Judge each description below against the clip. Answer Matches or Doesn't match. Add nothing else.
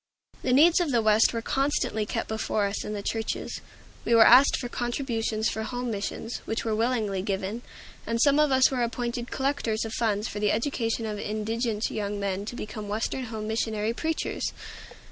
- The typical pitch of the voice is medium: Doesn't match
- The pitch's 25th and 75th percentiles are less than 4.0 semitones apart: Matches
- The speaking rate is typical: Matches